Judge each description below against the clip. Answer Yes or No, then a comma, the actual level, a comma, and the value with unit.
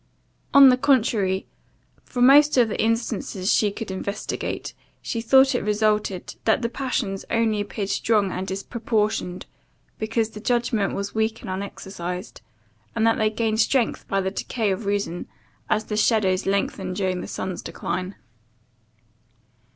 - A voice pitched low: No, high, 215 Hz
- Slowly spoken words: No, average, 145 wpm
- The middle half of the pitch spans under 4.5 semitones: Yes, average, 2.9 semitones